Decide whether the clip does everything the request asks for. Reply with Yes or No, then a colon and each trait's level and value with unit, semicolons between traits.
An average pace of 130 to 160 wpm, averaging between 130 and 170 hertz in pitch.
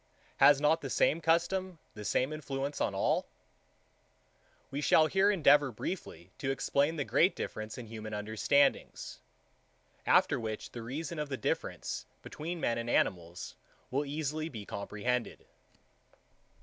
Yes: slow, 135 wpm; medium, 140 Hz